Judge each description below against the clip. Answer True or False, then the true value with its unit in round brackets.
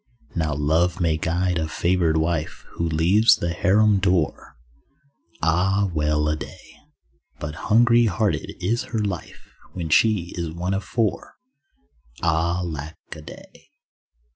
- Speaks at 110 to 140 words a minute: True (135 wpm)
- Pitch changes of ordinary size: True (3.5 semitones)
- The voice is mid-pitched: False (85 Hz)